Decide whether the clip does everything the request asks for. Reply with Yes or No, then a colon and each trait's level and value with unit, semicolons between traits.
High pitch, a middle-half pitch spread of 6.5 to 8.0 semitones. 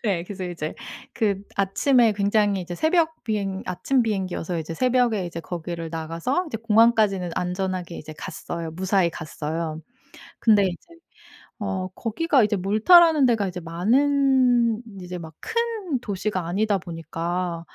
No: high, 195 Hz; average, 5.2 semitones